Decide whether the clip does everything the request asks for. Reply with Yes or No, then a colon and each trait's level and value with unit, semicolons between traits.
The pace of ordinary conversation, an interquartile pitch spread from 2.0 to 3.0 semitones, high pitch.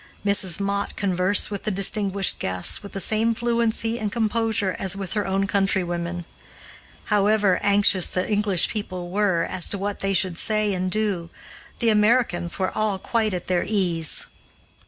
Yes: average, 160 wpm; narrow, 2.5 semitones; high, 200 Hz